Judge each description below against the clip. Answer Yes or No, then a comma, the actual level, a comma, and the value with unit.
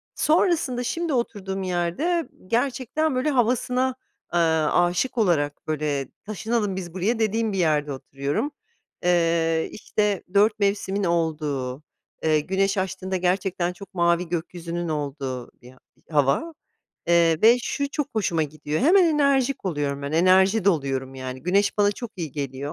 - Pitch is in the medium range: Yes, medium, 180 Hz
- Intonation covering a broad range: Yes, wide, 6.3 semitones